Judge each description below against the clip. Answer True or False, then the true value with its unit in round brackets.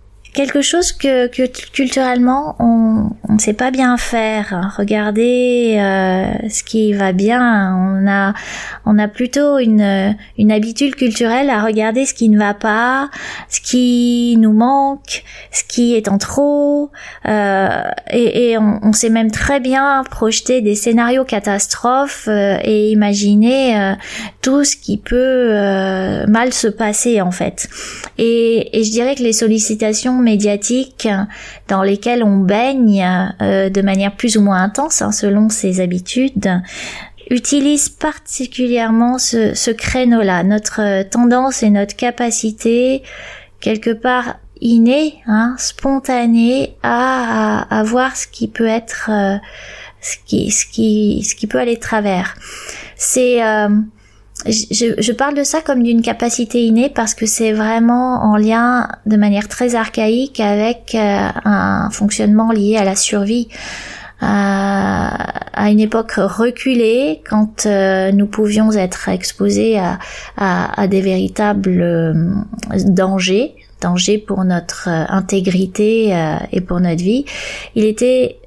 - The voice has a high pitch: True (225 Hz)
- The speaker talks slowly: True (140 wpm)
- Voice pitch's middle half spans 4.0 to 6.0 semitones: False (3.3 semitones)